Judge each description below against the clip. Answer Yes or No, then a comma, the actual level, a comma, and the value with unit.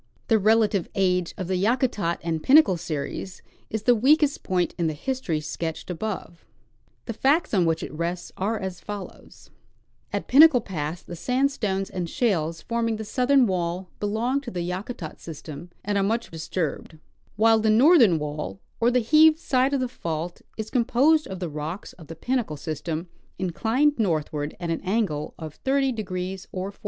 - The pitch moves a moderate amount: No, wide, 6.1 semitones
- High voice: Yes, high, 195 Hz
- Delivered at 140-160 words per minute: No, average, 170 wpm